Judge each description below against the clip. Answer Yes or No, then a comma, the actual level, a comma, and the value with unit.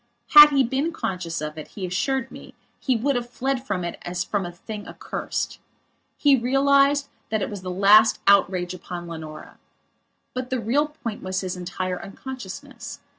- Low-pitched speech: No, high, 215 Hz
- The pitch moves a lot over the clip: Yes, wide, 6.6 semitones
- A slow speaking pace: No, average, 175 wpm